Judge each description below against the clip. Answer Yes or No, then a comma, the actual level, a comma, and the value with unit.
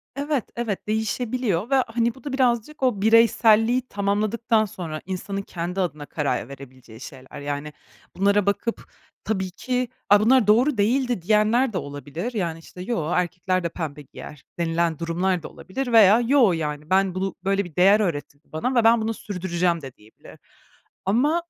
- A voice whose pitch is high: Yes, high, 195 Hz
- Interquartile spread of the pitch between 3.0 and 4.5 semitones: No, wide, 5.6 semitones